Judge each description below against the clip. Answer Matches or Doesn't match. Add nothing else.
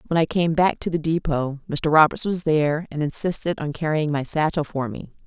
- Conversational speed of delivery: Doesn't match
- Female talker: Matches